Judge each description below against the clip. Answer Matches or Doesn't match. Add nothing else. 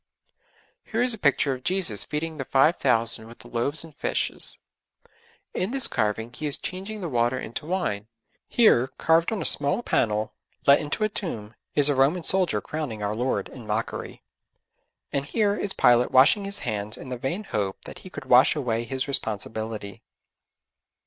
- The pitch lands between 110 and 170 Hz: Matches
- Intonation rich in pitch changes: Matches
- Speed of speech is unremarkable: Matches